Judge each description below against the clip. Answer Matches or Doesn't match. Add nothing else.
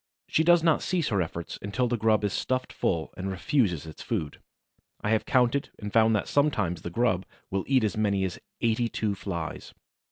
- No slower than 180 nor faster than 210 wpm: Matches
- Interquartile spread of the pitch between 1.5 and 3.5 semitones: Doesn't match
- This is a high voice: Doesn't match